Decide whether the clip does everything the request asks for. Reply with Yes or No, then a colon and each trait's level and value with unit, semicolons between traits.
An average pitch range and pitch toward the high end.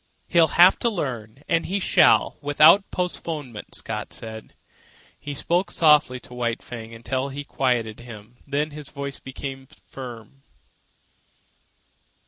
No: average, 4.1 semitones; low, 135 Hz